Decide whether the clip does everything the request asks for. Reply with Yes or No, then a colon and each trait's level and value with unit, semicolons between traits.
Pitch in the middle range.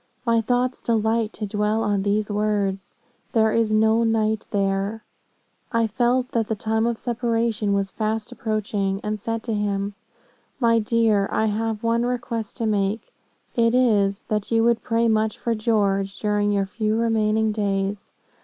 No: high, 220 Hz